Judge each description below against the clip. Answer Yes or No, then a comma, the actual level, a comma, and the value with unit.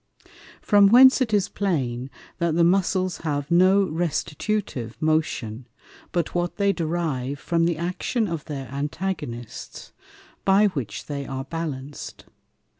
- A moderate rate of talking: No, slow, 125 wpm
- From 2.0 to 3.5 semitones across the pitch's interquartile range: No, average, 5.3 semitones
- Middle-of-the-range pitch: Yes, medium, 165 Hz